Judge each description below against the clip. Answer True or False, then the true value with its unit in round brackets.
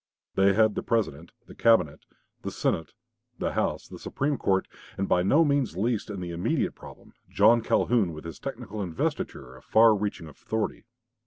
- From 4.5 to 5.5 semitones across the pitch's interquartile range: True (5.1 semitones)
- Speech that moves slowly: False (170 wpm)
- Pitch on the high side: False (100 Hz)